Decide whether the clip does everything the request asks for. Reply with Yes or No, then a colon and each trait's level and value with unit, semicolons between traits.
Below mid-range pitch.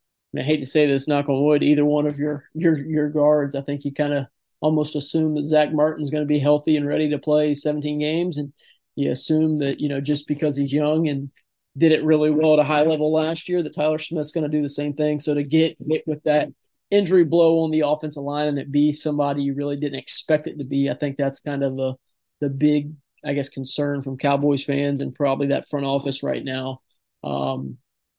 No: medium, 150 Hz